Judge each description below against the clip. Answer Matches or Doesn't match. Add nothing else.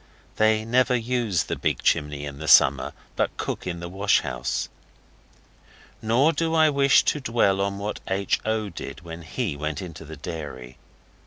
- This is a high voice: Doesn't match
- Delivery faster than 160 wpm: Matches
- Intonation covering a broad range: Matches